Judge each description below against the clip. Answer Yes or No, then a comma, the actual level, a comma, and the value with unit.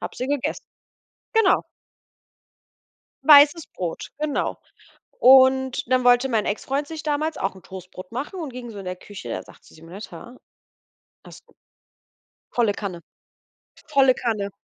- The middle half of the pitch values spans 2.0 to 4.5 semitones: No, wide, 6.2 semitones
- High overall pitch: Yes, very high, 250 Hz